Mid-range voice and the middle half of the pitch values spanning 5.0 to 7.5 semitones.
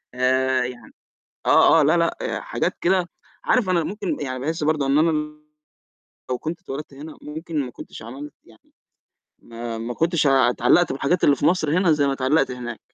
No: medium, 145 Hz; average, 4.2 semitones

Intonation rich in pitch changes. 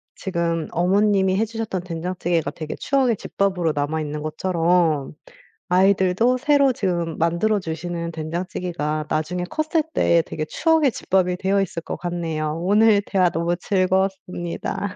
No: average, 3.1 semitones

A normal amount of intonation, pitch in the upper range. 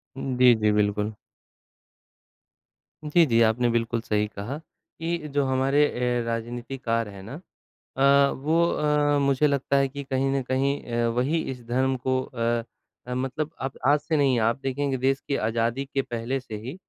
No: average, 3.0 semitones; low, 130 Hz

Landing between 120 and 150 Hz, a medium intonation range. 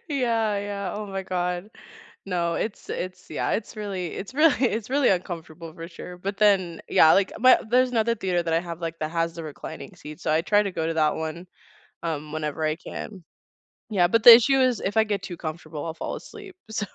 No: medium, 185 Hz; average, 4.5 semitones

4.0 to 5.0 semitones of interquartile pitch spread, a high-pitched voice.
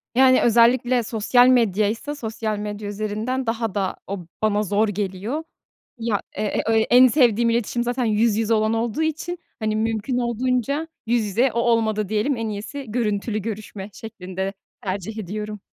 No: narrow, 2.5 semitones; high, 220 Hz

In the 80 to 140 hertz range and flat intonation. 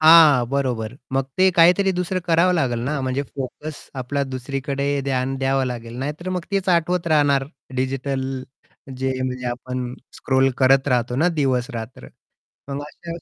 No: low, 135 Hz; average, 3.3 semitones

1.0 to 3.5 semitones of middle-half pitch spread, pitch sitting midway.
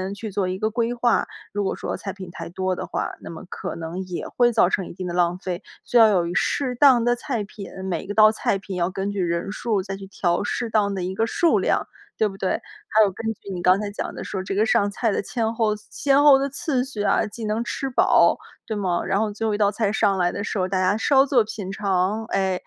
No: average, 3.1 semitones; high, 205 Hz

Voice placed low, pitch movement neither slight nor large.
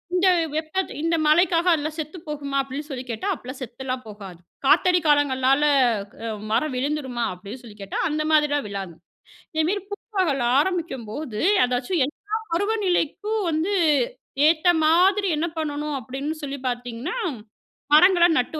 No: very high, 300 Hz; average, 5.0 semitones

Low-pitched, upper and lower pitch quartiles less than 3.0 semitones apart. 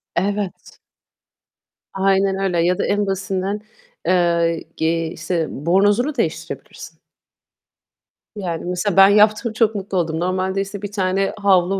No: high, 190 Hz; narrow, 2.5 semitones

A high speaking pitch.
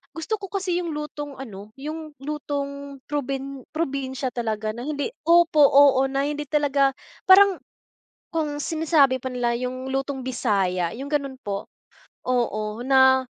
Yes: very high, 275 Hz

